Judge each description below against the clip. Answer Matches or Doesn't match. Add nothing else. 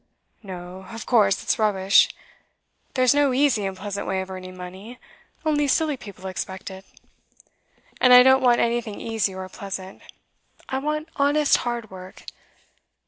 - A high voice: Matches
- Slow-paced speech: Doesn't match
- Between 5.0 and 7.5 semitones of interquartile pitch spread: Matches